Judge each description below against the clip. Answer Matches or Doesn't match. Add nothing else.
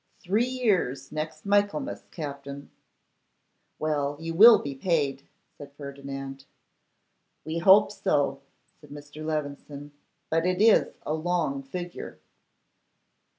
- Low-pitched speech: Doesn't match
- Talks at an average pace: Doesn't match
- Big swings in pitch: Doesn't match